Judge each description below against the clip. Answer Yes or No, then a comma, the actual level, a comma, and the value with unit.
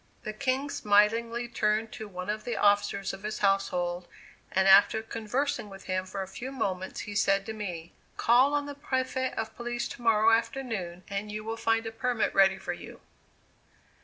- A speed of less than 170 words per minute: No, average, 185 wpm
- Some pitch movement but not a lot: Yes, average, 3.3 semitones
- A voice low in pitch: No, high, 215 Hz